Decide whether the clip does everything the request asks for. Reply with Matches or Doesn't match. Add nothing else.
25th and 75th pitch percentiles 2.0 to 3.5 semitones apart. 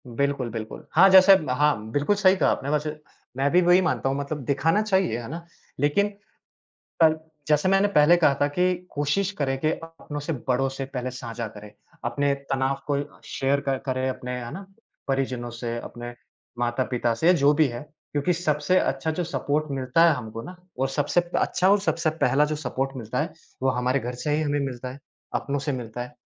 Doesn't match